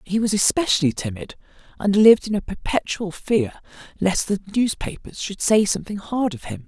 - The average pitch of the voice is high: Yes, high, 205 Hz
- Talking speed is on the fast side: No, average, 170 wpm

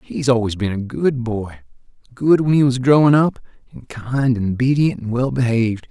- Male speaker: Yes, male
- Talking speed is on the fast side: No, average, 185 wpm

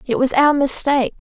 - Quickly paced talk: No, average, 175 wpm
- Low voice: No, very high, 270 Hz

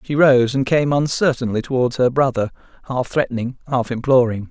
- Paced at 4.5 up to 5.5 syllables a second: Yes, 5.4 syllables/s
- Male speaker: Yes, male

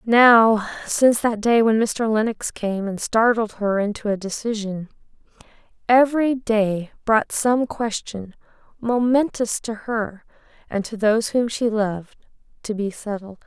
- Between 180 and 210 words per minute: No, average, 140 wpm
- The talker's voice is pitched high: Yes, high, 220 Hz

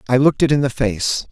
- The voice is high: No, low, 130 Hz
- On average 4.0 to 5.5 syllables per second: No, 6.4 syllables/s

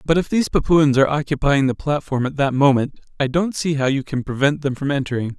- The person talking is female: No, male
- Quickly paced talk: Yes, fast, 235 wpm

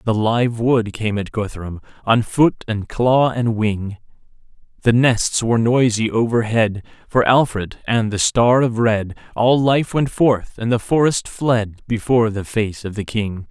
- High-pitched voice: No, low, 115 Hz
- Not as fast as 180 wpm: Yes, average, 170 wpm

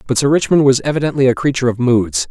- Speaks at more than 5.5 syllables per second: Yes, 6.9 syllables/s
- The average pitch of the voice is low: Yes, low, 130 Hz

